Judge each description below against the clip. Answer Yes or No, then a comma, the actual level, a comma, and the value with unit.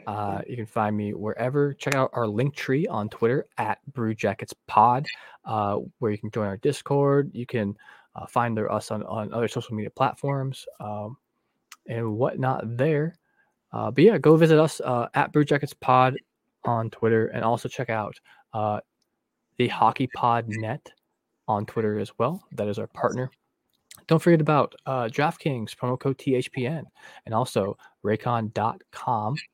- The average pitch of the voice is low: Yes, low, 120 Hz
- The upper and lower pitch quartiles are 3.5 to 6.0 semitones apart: Yes, average, 4.3 semitones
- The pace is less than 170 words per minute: Yes, average, 160 wpm